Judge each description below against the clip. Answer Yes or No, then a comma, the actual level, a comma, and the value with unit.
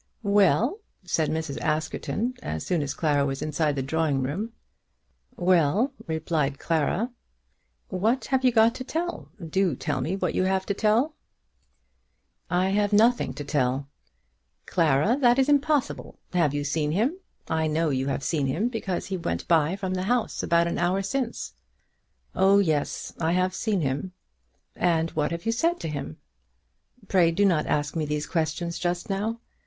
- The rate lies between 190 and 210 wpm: No, average, 165 wpm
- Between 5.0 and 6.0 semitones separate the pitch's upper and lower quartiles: Yes, wide, 5.6 semitones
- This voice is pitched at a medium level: Yes, medium, 175 Hz